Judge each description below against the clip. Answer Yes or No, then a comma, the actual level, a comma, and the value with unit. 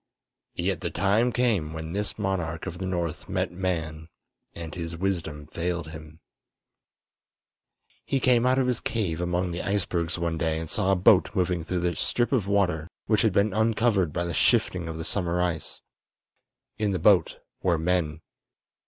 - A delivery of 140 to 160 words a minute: No, average, 170 wpm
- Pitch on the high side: No, very low, 90 Hz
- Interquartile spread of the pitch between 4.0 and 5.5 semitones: No, average, 3.5 semitones